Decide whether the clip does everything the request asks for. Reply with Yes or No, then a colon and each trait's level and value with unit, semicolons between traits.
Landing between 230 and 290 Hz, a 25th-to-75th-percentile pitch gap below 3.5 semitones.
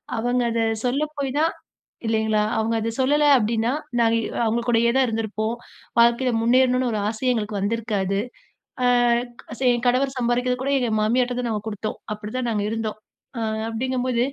Yes: high, 235 Hz; narrow, 2.4 semitones